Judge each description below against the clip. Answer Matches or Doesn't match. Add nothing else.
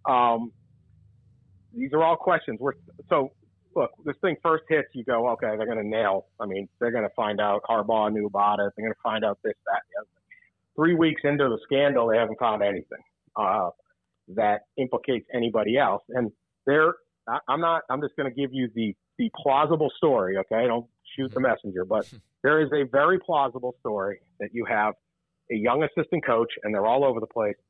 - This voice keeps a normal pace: Matches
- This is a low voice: Matches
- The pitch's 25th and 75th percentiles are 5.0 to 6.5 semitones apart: Matches